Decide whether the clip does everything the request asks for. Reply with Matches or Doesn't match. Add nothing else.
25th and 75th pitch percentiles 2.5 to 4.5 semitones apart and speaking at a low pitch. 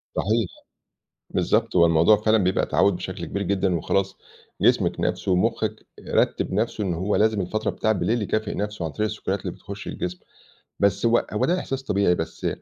Matches